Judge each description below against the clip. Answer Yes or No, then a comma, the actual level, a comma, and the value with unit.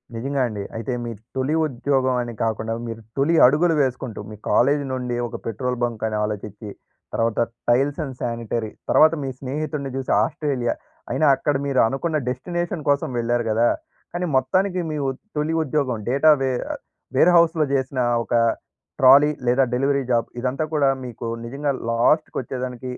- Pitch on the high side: No, low, 130 Hz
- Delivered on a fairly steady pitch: No, average, 3.7 semitones